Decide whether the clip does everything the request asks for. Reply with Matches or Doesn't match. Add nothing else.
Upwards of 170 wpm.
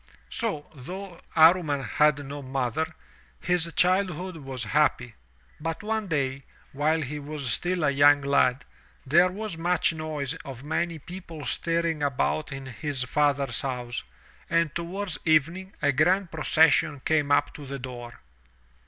Doesn't match